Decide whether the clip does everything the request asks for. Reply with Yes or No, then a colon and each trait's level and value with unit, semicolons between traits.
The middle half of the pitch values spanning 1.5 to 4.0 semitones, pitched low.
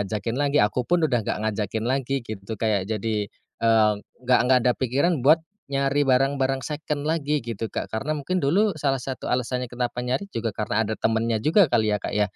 No: average, 4.4 semitones; low, 125 Hz